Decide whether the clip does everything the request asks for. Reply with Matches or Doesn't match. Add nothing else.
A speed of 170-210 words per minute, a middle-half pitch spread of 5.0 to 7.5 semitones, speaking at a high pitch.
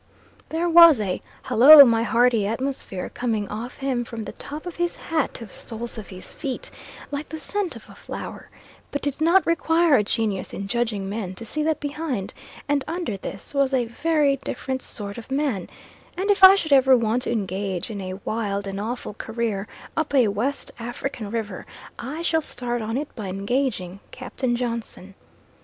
Matches